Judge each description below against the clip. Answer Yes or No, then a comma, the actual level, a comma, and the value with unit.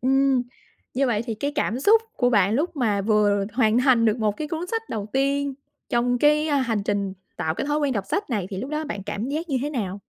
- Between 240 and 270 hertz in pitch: Yes, very high, 250 Hz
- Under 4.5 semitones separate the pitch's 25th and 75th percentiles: No, average, 5.3 semitones